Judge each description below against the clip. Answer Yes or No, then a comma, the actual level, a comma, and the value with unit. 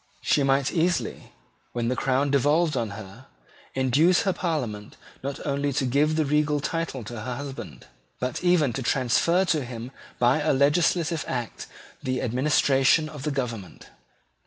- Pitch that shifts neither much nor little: Yes, average, 3.5 semitones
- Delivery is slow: No, average, 155 wpm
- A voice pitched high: No, medium, 140 Hz